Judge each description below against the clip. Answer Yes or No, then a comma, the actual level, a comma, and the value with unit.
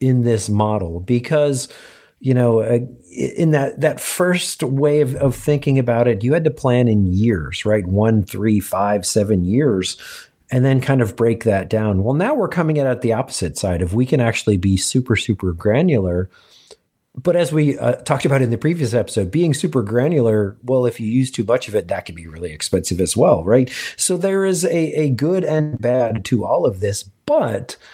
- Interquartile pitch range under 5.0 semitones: No, wide, 5.6 semitones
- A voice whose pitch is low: Yes, low, 120 Hz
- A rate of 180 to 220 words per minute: Yes, average, 200 wpm